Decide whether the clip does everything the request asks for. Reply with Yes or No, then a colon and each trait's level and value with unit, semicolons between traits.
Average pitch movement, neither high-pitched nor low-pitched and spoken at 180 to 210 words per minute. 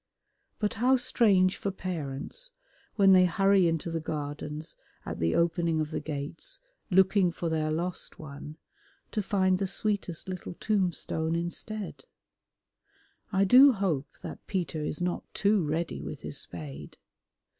No: average, 4.1 semitones; medium, 175 Hz; average, 140 wpm